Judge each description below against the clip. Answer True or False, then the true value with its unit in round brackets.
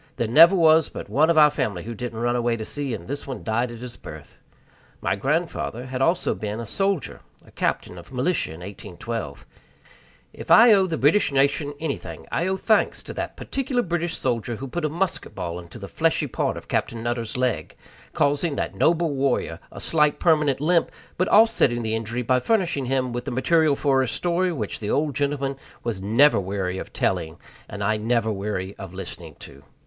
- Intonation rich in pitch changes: True (6.3 semitones)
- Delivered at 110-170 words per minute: False (200 wpm)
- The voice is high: False (130 Hz)